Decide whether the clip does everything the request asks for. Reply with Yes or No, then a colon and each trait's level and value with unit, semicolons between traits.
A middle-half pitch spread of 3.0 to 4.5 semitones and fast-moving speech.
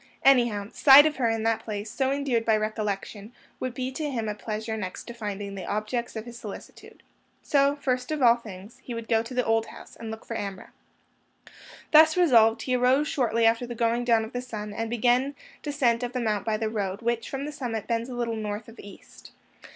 No: narrow, 2.6 semitones; fast, 220 wpm